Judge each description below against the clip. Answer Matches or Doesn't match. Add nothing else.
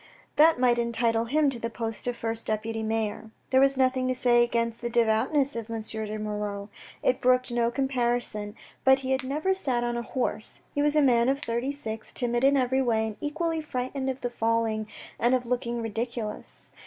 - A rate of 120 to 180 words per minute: Doesn't match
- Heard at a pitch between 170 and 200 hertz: Doesn't match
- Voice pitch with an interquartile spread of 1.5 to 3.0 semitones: Matches